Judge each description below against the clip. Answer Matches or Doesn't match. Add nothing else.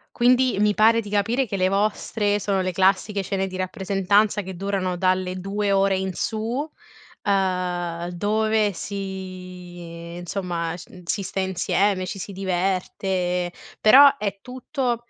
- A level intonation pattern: Matches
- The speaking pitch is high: Matches